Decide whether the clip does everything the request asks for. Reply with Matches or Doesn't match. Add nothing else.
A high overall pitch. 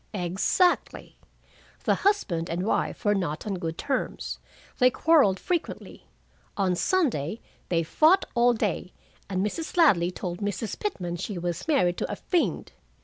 Matches